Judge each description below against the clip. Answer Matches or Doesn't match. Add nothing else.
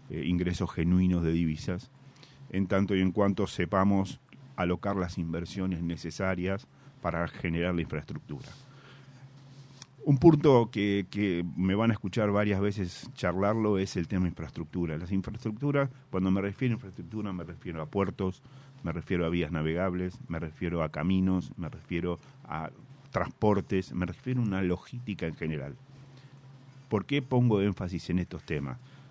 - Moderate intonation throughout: Doesn't match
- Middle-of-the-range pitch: Doesn't match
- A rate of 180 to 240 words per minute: Doesn't match